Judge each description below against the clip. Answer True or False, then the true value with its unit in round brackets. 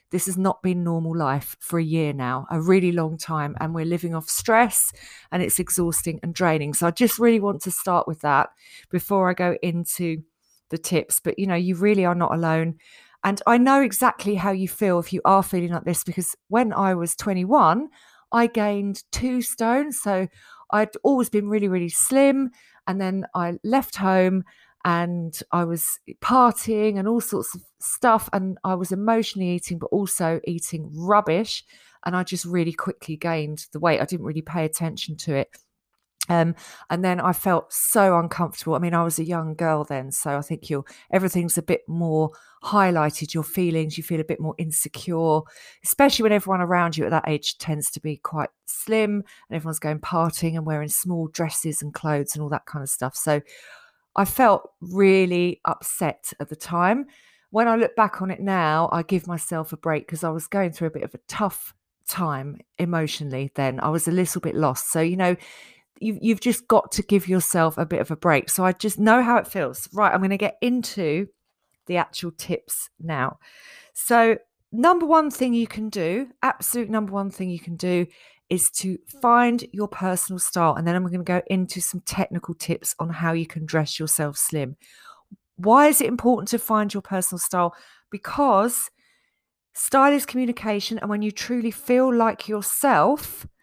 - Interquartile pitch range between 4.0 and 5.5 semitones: True (4.4 semitones)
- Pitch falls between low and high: True (180 Hz)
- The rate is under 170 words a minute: False (195 wpm)